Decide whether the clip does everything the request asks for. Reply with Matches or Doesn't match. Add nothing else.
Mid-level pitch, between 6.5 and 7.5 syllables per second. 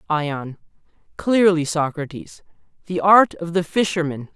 Doesn't match